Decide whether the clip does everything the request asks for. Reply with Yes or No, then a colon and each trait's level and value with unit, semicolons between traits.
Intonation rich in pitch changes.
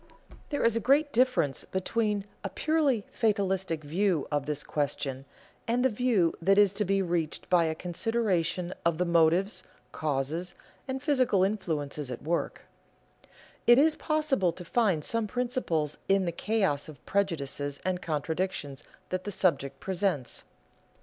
Yes: wide, 5.9 semitones